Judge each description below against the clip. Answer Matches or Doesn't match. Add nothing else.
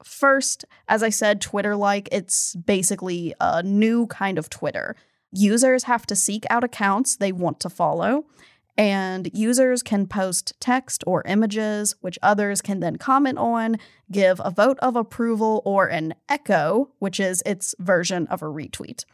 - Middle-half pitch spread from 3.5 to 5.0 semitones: Matches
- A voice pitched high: Matches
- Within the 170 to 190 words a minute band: Doesn't match